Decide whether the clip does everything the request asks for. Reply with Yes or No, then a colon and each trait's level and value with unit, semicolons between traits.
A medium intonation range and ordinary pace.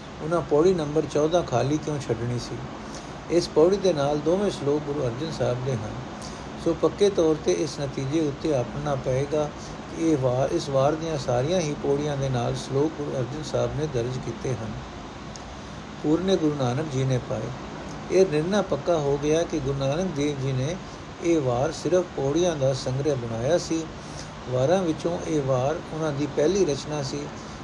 No: average, 3.7 semitones; fast, 175 wpm